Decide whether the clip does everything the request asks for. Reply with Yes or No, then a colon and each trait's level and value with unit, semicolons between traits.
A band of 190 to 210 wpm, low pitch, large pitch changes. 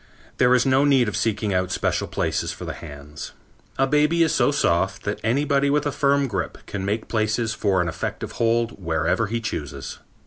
Yes: average, 195 wpm; low, 115 Hz; wide, 6.3 semitones